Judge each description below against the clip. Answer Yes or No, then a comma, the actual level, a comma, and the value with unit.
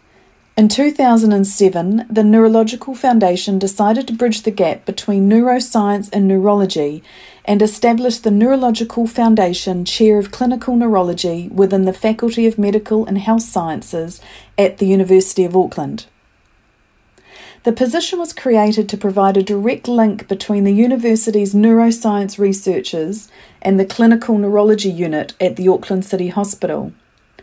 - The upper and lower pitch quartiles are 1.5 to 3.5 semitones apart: Yes, average, 2.9 semitones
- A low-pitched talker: No, high, 210 Hz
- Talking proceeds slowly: Yes, slow, 130 wpm